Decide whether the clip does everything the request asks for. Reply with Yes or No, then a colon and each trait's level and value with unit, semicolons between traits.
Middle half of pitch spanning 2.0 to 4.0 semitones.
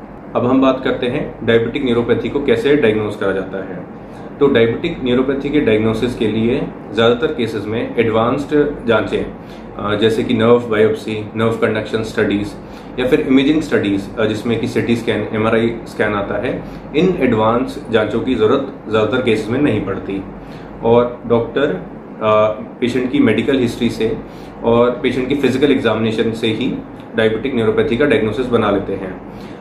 Yes: narrow, 2.6 semitones